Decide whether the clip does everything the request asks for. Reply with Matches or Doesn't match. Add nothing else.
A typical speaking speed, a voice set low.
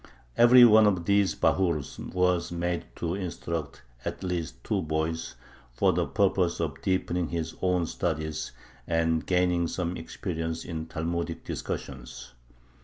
Doesn't match